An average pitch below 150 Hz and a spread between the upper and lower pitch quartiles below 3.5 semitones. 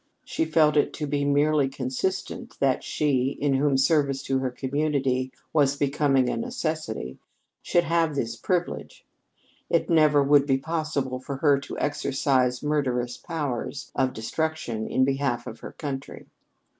Yes: medium, 140 Hz; narrow, 2.5 semitones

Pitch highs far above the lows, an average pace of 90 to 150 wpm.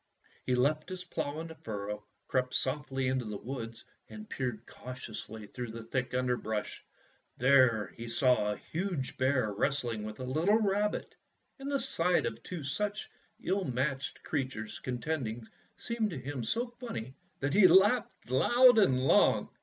No: wide, 7.0 semitones; average, 160 wpm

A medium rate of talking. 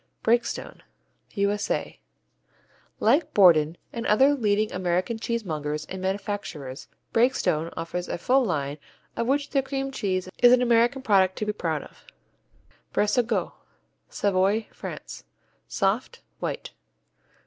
No: slow, 115 wpm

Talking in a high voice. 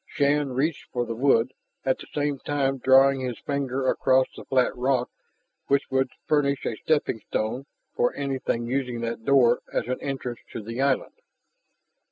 No: low, 130 Hz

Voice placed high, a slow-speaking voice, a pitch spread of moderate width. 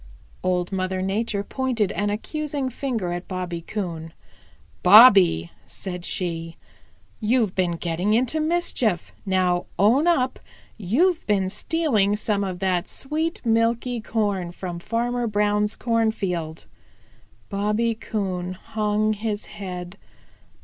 Yes: high, 205 Hz; slow, 115 wpm; average, 4.2 semitones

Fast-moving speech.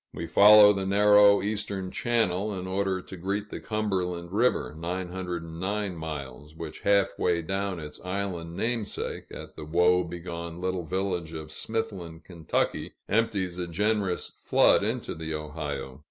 No: average, 145 wpm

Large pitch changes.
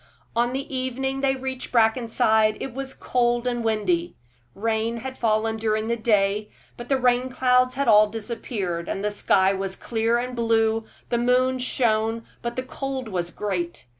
No: average, 2.8 semitones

